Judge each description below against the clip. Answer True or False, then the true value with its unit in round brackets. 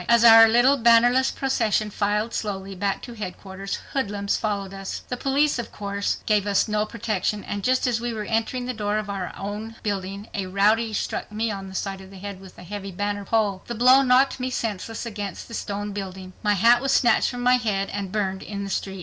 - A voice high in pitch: True (210 Hz)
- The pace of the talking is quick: True (220 wpm)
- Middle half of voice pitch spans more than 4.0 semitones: False (2.9 semitones)